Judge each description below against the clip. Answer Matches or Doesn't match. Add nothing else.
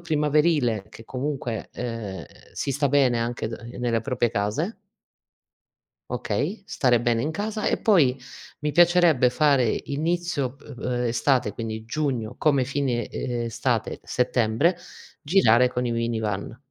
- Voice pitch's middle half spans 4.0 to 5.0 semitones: Matches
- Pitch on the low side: Matches